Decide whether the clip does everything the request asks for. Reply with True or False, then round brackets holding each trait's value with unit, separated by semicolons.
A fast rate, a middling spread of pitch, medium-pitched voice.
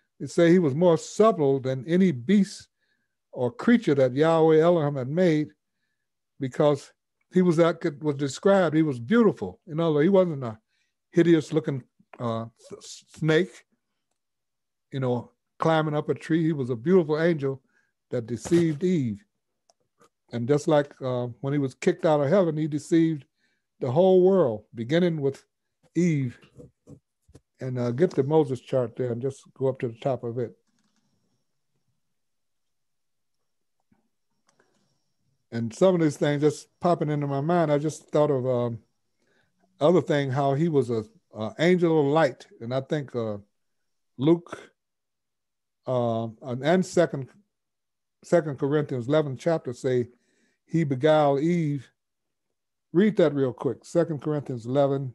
False (145 wpm; 4.6 semitones; 150 Hz)